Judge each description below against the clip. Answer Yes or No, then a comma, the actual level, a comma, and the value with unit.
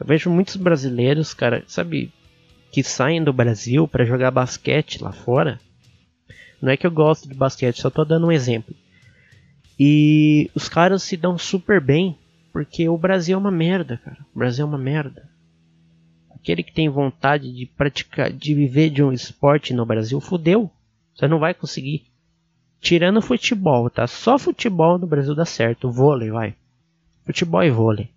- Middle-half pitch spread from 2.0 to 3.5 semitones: No, average, 4.8 semitones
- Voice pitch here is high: No, medium, 145 Hz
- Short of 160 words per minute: No, average, 175 wpm